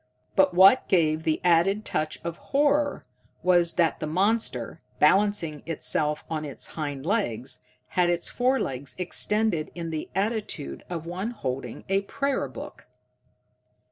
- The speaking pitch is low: No, medium, 175 Hz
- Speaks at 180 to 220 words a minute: No, slow, 135 wpm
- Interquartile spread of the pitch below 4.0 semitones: No, average, 4.9 semitones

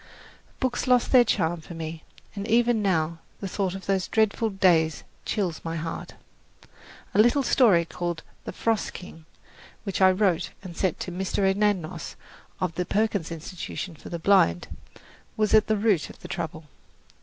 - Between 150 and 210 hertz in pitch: Yes, high, 190 Hz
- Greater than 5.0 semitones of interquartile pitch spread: No, average, 4.1 semitones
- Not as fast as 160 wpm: No, average, 165 wpm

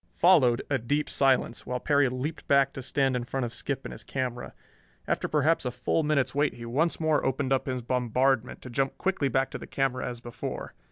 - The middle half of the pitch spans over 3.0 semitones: No, narrow, 2.4 semitones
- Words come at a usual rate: No, fast, 215 wpm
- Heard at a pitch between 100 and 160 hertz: Yes, low, 135 Hz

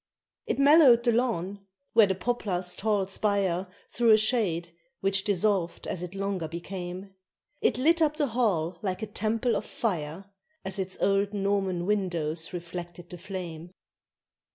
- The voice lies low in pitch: No, high, 195 Hz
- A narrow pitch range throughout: No, average, 3.5 semitones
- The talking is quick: No, average, 150 wpm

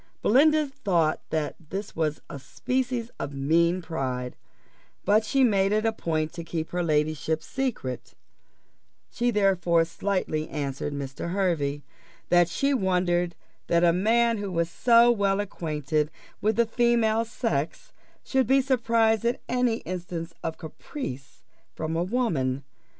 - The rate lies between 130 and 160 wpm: Yes, average, 140 wpm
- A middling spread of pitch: No, wide, 6.6 semitones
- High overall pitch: No, medium, 180 Hz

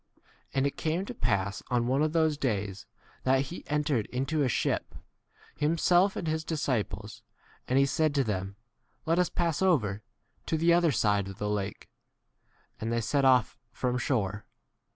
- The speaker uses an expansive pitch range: Yes, wide, 6.9 semitones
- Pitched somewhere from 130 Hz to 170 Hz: Yes, low, 135 Hz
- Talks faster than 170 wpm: Yes, average, 185 wpm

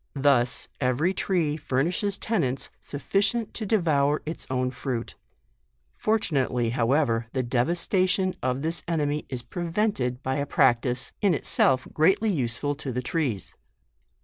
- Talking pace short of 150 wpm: Yes, slow, 135 wpm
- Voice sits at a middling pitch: Yes, medium, 145 Hz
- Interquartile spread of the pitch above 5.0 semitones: Yes, wide, 5.5 semitones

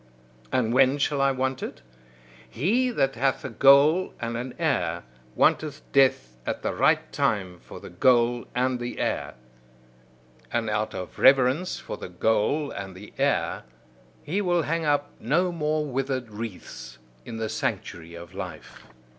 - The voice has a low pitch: Yes, low, 130 Hz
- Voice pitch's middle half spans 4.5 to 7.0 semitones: Yes, average, 5.0 semitones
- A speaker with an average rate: Yes, average, 155 wpm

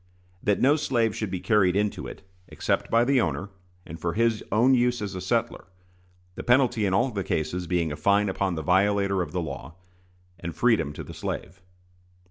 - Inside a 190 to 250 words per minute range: Yes, average, 195 wpm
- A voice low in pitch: Yes, low, 100 Hz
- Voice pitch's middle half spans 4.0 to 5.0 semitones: Yes, average, 4.7 semitones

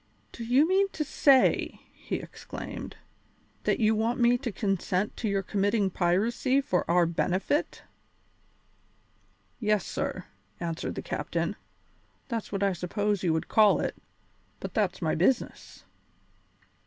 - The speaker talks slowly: Yes, slow, 130 wpm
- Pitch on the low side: No, high, 205 Hz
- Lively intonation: No, average, 4.5 semitones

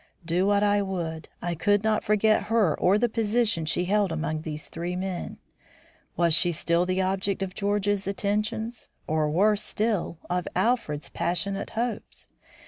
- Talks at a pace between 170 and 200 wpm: No, average, 155 wpm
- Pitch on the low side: No, high, 195 Hz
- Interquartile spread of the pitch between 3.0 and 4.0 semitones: Yes, average, 3.5 semitones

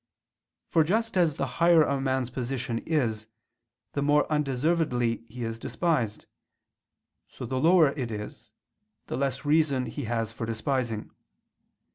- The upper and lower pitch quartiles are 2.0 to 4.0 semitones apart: No, average, 4.7 semitones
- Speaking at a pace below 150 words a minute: Yes, slow, 135 wpm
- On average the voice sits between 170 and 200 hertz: No, low, 135 Hz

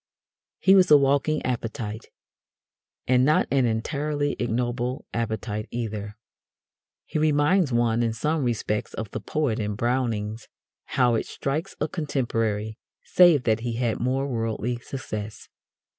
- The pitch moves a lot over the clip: No, average, 4.3 semitones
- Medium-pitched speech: No, low, 120 Hz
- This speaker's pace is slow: Yes, slow, 130 wpm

